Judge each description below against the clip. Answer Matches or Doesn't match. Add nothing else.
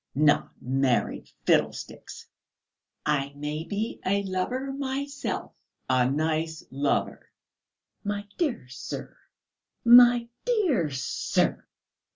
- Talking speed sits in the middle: Doesn't match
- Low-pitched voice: Doesn't match